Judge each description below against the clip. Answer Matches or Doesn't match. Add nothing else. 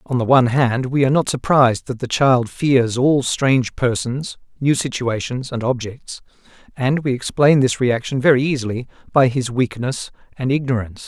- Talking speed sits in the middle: Matches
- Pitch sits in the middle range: Doesn't match